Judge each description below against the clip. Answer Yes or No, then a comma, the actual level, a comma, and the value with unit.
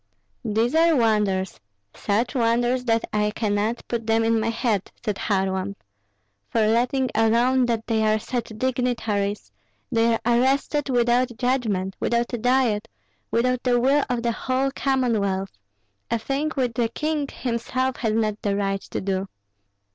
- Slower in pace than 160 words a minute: Yes, average, 150 wpm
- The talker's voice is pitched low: No, high, 230 Hz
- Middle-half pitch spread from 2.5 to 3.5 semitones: Yes, average, 2.8 semitones